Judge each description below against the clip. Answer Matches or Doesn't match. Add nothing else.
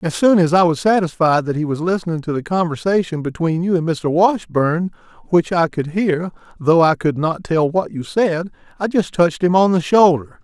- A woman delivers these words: Doesn't match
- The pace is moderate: Doesn't match